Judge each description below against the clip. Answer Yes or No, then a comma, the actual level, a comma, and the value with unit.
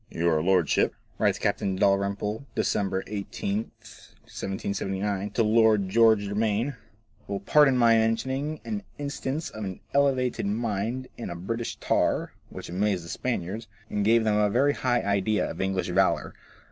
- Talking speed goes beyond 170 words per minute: No, average, 145 wpm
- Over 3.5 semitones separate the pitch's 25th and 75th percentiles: No, average, 3.2 semitones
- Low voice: Yes, low, 105 Hz